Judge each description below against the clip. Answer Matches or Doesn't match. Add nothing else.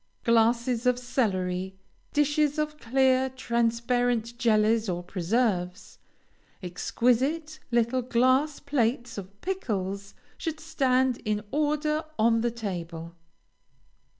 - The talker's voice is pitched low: Doesn't match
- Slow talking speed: Matches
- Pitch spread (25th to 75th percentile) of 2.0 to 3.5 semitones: Doesn't match